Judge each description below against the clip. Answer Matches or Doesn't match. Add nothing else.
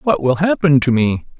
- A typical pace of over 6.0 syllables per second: Doesn't match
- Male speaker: Matches